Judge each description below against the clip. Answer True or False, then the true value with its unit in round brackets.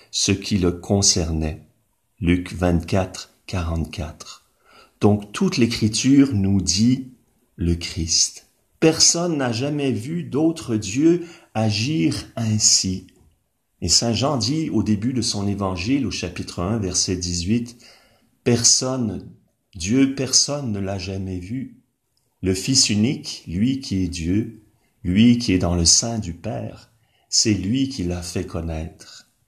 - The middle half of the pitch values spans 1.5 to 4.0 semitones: False (4.9 semitones)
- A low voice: True (110 Hz)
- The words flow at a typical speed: False (130 wpm)